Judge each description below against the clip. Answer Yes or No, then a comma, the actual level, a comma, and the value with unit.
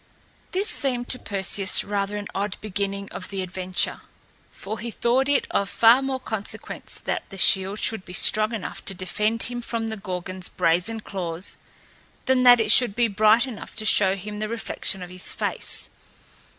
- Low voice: No, high, 210 Hz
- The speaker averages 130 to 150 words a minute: No, average, 175 wpm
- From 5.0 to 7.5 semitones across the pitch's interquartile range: No, average, 3.3 semitones